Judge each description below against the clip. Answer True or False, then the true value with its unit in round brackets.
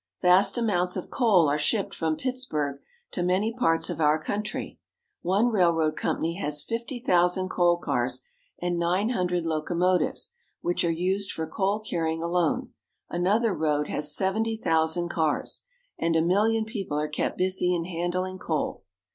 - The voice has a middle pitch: True (180 Hz)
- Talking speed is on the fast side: False (155 wpm)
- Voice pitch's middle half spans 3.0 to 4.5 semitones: True (3.5 semitones)